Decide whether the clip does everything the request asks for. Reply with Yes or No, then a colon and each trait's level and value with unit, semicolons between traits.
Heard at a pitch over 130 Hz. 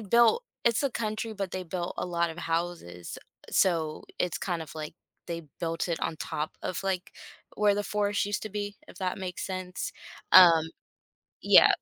Yes: medium, 185 Hz